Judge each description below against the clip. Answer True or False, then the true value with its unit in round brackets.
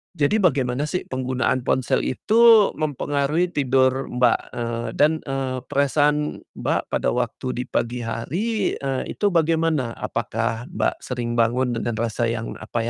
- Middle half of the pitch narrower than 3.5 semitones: False (4.1 semitones)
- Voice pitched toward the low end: True (130 Hz)